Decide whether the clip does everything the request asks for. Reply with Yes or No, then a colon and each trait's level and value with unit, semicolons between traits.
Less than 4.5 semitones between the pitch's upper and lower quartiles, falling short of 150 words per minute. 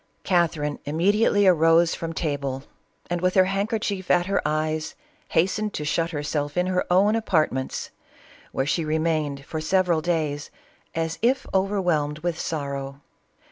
Yes: average, 3.7 semitones; average, 140 wpm